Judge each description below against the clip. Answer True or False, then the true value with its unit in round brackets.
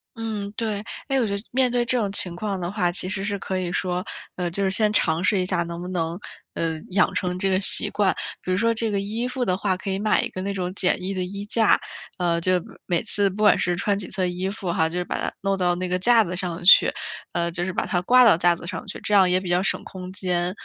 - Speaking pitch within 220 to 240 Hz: False (185 Hz)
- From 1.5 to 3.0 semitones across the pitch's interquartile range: True (2.4 semitones)